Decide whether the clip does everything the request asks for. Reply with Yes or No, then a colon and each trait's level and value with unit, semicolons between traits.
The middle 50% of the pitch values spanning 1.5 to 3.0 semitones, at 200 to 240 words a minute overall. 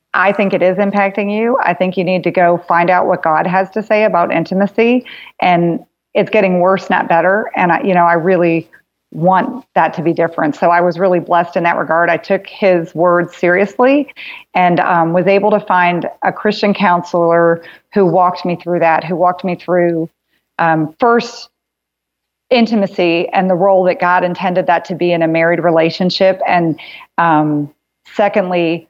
No: narrow, 2.5 semitones; average, 185 wpm